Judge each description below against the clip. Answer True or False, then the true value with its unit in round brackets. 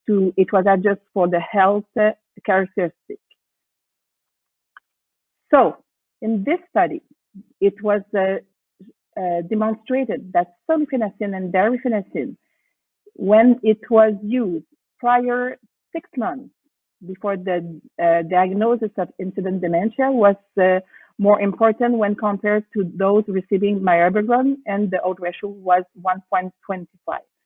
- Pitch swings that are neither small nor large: True (3.7 semitones)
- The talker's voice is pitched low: False (205 Hz)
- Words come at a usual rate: False (115 wpm)